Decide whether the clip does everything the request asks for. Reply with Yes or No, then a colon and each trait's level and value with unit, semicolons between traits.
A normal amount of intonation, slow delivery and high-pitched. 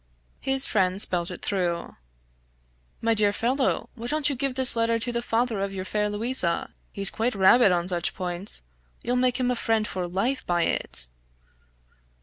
No: average, 4.8 semitones; average, 175 wpm; high, 220 Hz